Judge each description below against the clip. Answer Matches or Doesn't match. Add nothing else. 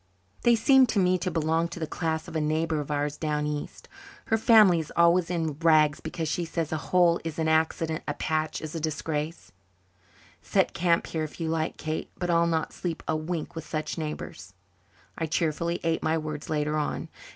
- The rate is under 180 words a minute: Doesn't match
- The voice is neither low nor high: Matches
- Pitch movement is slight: Matches